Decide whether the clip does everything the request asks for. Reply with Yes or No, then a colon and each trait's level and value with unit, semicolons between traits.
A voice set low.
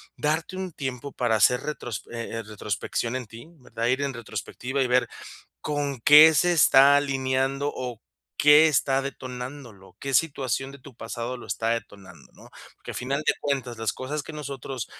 Yes: low, 130 Hz